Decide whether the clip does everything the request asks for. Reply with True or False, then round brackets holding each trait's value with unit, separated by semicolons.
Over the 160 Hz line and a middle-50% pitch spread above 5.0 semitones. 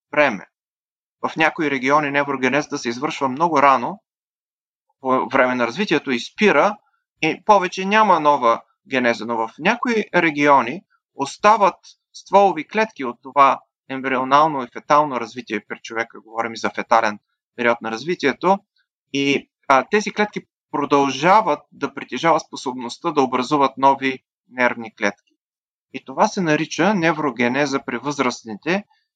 False (140 Hz; 5.4 semitones)